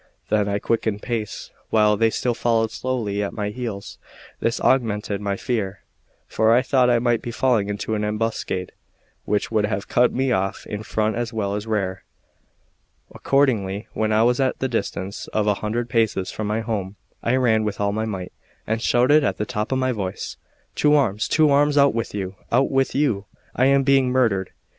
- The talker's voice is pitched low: Yes, low, 110 Hz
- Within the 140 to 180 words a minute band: No, average, 195 wpm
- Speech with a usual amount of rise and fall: Yes, average, 3.4 semitones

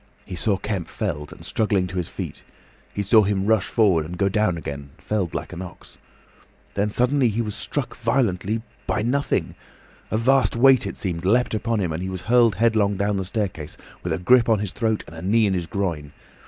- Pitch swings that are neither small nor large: Yes, average, 3.9 semitones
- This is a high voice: No, low, 100 Hz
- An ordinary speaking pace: No, fast, 210 wpm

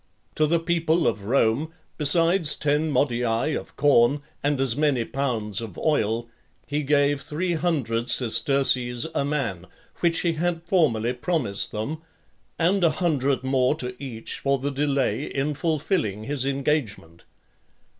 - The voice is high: No, medium, 140 Hz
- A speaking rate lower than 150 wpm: Yes, average, 140 wpm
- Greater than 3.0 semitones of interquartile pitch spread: Yes, average, 4.4 semitones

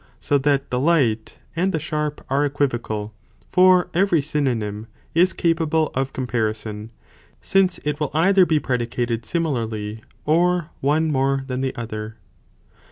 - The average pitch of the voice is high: No, medium, 140 Hz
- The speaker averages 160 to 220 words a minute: No, slow, 135 wpm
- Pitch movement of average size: No, wide, 5.7 semitones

